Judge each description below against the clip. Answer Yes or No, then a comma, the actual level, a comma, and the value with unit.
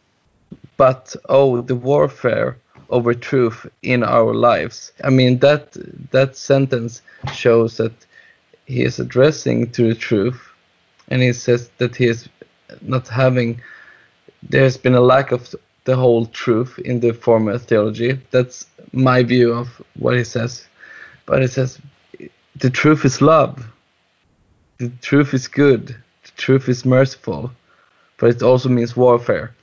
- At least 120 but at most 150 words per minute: Yes, average, 140 wpm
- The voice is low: Yes, low, 125 Hz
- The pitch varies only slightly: Yes, narrow, 1.9 semitones